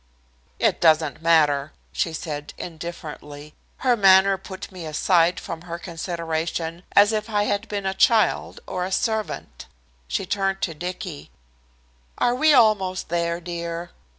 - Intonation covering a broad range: No, average, 3.2 semitones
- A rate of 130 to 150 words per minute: Yes, average, 140 wpm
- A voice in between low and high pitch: Yes, medium, 175 Hz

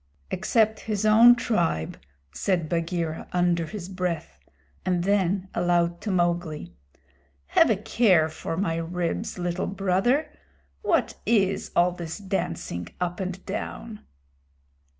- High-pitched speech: No, medium, 180 Hz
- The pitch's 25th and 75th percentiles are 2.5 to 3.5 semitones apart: Yes, average, 3.0 semitones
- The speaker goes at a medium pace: No, slow, 120 wpm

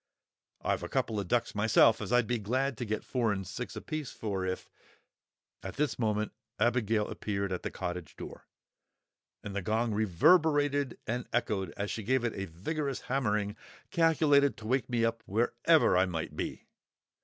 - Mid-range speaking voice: No, low, 115 Hz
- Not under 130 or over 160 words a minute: No, average, 170 wpm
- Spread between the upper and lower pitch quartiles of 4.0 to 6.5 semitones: Yes, average, 4.4 semitones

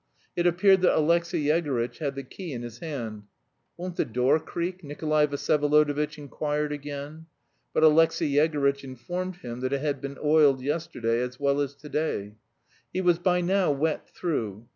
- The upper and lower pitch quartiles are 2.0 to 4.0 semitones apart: Yes, average, 3.1 semitones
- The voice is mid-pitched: Yes, medium, 150 Hz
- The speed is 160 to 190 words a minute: Yes, average, 165 wpm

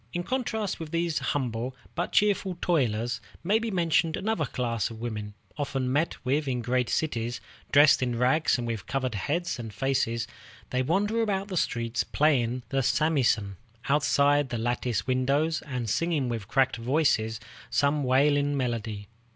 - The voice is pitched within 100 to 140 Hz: Yes, low, 135 Hz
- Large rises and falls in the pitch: No, average, 4.9 semitones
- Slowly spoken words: No, average, 160 wpm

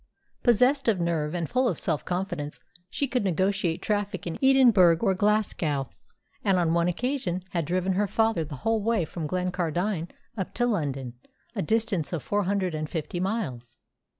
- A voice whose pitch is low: No, medium, 185 Hz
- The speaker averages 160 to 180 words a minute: Yes, average, 170 wpm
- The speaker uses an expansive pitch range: No, average, 4.6 semitones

